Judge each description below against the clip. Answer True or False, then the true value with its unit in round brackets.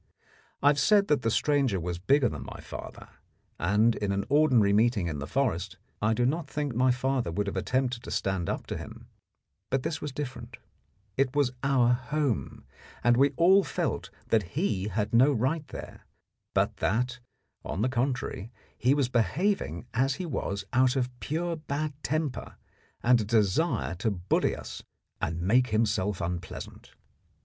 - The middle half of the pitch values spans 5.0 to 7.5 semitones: True (5.4 semitones)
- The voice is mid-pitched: False (125 Hz)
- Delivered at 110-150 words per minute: False (170 wpm)